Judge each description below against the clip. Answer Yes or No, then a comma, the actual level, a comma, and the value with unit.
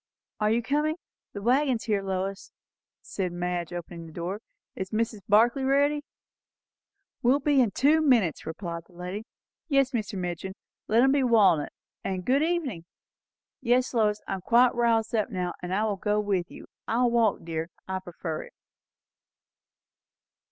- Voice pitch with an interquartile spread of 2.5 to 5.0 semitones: No, wide, 5.5 semitones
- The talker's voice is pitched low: No, high, 210 Hz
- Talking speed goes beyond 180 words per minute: No, average, 160 wpm